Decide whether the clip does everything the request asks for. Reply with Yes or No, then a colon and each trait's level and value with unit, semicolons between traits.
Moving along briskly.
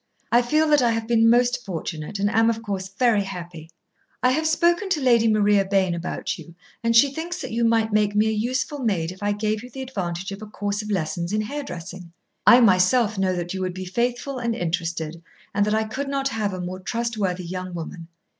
Yes: fast, 220 wpm